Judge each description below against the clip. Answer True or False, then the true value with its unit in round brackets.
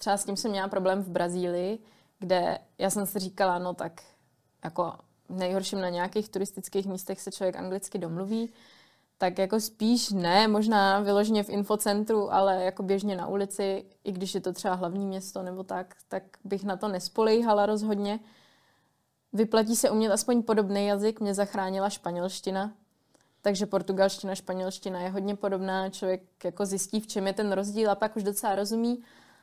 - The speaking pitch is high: True (200 Hz)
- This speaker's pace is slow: False (165 wpm)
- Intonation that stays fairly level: True (1.8 semitones)